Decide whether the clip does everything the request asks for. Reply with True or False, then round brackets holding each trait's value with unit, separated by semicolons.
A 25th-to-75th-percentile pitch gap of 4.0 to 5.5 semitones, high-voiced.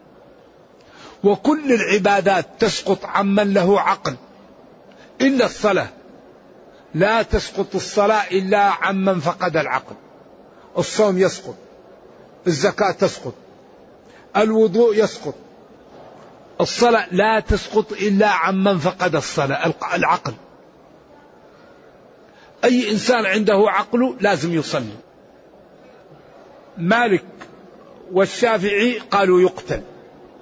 False (2.5 semitones; 205 Hz)